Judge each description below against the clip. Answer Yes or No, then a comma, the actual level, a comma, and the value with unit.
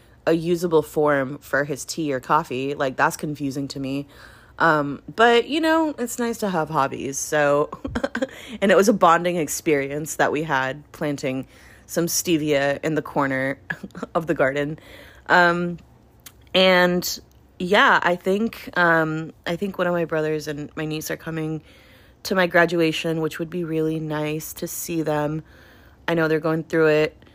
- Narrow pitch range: No, average, 3.3 semitones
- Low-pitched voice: No, medium, 155 Hz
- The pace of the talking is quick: No, average, 165 wpm